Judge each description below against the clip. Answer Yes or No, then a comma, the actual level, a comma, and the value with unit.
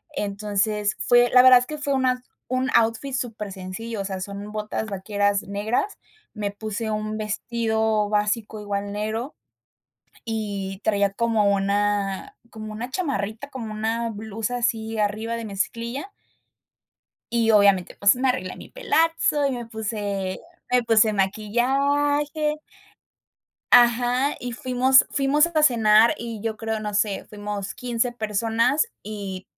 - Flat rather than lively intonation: No, average, 3.1 semitones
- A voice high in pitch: Yes, high, 220 Hz